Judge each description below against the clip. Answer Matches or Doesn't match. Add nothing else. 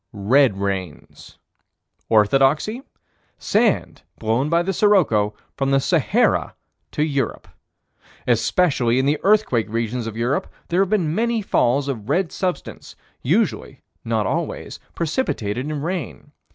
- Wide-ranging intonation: Matches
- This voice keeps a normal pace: Doesn't match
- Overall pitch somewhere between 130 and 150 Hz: Matches